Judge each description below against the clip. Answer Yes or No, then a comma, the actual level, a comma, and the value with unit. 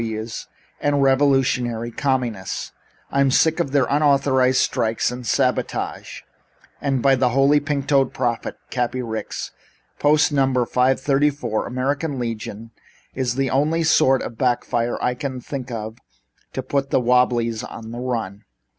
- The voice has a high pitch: No, low, 130 Hz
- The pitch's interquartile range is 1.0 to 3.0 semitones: Yes, average, 2.7 semitones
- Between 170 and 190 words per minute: No, average, 140 wpm